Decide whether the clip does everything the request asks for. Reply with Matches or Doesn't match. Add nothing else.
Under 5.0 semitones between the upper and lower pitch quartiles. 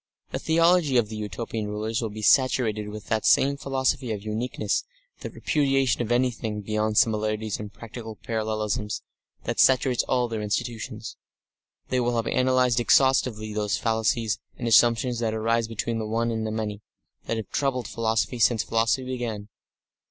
Matches